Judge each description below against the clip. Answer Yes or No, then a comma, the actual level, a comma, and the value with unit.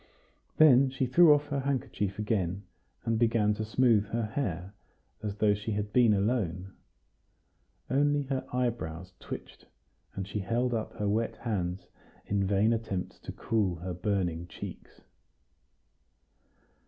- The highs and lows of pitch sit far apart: No, average, 4.0 semitones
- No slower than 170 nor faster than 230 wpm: No, slow, 135 wpm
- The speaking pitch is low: Yes, low, 105 Hz